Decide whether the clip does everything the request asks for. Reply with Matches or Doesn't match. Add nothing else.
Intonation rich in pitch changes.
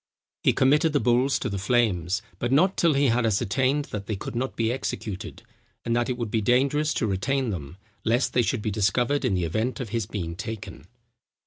Doesn't match